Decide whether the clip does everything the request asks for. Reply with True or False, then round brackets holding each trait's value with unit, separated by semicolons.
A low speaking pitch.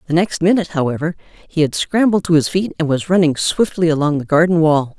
False (165 Hz)